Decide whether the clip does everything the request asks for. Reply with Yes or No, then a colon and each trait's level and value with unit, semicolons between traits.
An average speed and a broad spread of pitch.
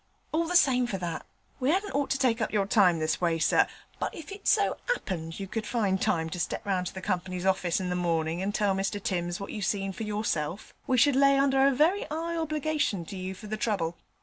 No: fast, 240 wpm; wide, 7.1 semitones